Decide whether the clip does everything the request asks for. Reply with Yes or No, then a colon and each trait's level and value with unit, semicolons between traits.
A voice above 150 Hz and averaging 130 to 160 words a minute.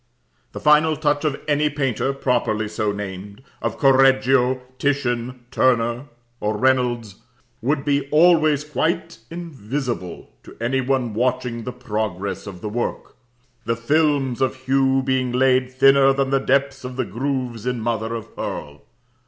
No: low, 130 Hz; average, 145 wpm